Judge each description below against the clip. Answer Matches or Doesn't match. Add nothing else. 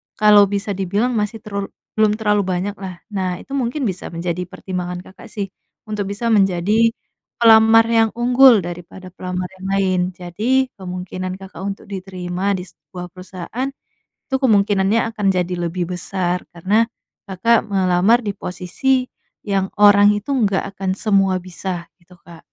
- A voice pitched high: Matches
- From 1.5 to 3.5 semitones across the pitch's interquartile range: Matches